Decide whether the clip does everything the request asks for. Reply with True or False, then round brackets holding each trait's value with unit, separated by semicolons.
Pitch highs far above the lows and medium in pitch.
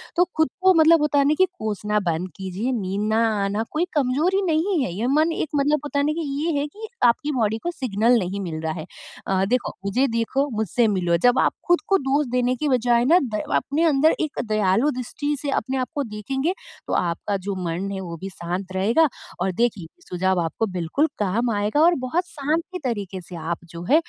False (7.5 semitones; 240 Hz)